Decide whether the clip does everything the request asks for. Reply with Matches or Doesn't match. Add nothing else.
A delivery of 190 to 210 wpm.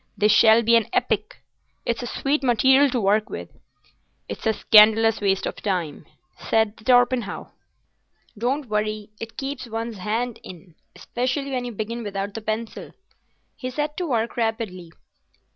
Doesn't match